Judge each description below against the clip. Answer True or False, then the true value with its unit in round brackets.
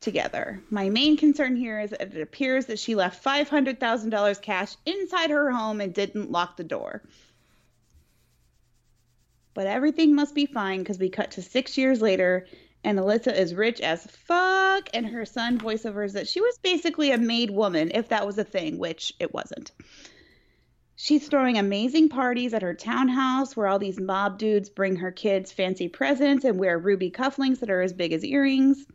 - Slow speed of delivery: False (185 wpm)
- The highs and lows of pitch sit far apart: True (5.8 semitones)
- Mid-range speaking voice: False (220 Hz)